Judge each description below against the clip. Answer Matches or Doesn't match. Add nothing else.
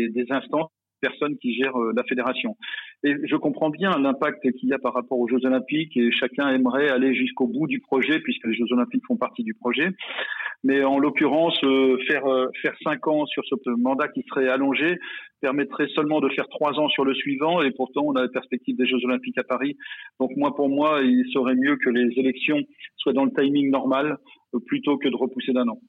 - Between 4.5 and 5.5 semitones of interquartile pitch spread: Doesn't match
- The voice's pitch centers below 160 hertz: Matches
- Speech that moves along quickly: Doesn't match